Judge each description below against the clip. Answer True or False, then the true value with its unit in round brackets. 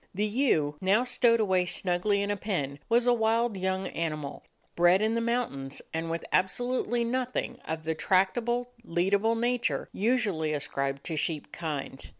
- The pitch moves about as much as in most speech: False (6.4 semitones)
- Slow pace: False (160 wpm)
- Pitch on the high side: True (195 Hz)